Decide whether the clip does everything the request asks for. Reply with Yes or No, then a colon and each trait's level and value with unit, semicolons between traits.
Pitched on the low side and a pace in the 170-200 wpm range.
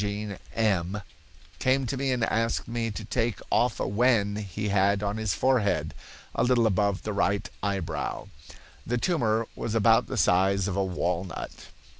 No: low, 105 Hz; average, 155 wpm